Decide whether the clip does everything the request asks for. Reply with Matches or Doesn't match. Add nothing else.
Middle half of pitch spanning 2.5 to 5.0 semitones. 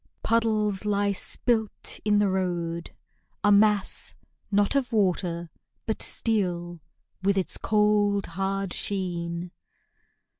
Matches